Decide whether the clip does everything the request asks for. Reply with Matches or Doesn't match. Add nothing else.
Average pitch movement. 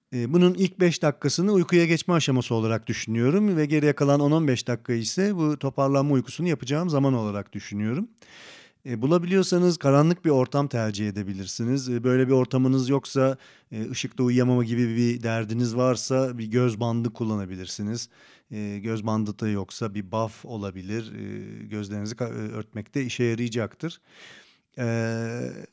Matches